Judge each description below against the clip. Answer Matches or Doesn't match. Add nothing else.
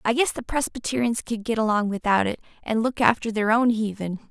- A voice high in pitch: Matches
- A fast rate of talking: Matches